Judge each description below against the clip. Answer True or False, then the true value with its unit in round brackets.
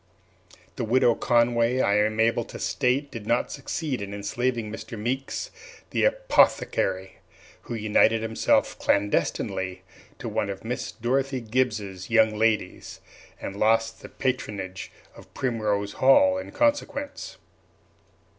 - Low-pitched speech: True (115 Hz)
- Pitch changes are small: False (3.6 semitones)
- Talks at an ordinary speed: False (125 wpm)